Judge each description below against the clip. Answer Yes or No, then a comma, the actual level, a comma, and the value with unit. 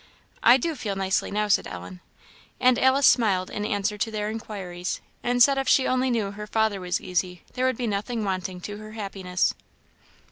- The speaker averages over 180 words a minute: Yes, average, 190 wpm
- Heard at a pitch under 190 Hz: No, high, 210 Hz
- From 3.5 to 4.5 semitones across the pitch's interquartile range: Yes, average, 4.2 semitones